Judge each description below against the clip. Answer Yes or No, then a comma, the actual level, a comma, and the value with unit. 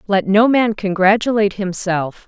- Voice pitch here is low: No, high, 200 Hz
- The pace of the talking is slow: Yes, slow, 130 wpm